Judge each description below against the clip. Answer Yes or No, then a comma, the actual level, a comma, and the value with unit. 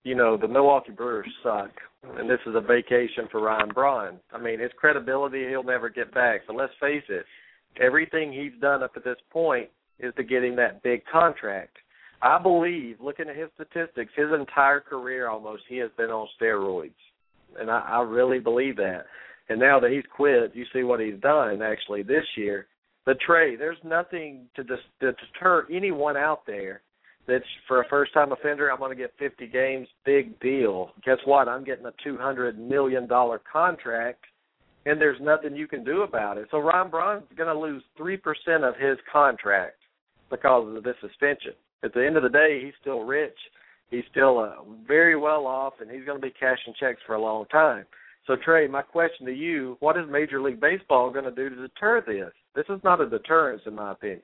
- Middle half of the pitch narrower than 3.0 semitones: No, average, 3.8 semitones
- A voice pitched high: No, low, 135 Hz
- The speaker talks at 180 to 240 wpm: Yes, average, 200 wpm